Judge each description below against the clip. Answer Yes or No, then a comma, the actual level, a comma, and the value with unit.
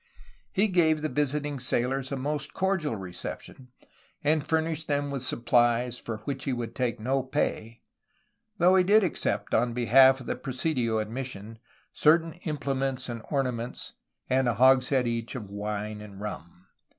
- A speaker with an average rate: Yes, average, 155 wpm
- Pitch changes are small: No, average, 4.0 semitones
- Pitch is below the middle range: Yes, low, 130 Hz